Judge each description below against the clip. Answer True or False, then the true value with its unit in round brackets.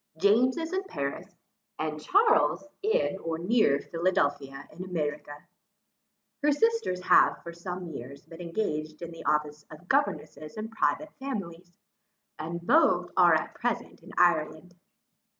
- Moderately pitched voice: True (175 Hz)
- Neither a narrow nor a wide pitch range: False (6.6 semitones)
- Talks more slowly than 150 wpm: True (135 wpm)